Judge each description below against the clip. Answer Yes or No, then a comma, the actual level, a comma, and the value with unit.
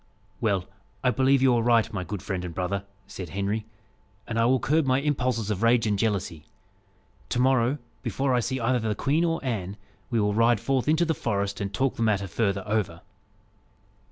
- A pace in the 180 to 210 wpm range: Yes, average, 195 wpm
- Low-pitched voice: Yes, low, 115 Hz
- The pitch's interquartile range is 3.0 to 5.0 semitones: Yes, average, 4.5 semitones